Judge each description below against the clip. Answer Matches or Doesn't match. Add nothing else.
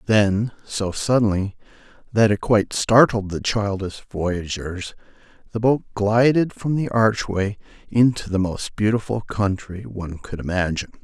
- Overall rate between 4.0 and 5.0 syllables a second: Matches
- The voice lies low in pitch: Matches